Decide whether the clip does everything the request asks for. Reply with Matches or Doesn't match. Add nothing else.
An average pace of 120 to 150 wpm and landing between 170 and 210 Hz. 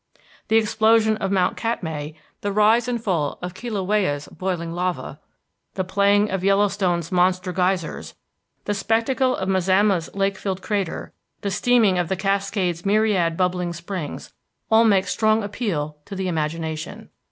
Matches